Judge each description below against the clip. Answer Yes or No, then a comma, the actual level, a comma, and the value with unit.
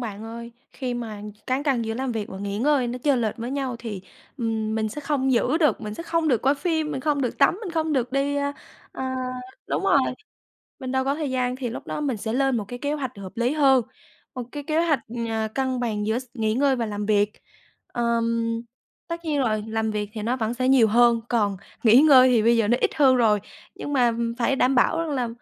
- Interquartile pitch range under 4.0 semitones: Yes, average, 3.6 semitones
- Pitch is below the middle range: No, high, 245 Hz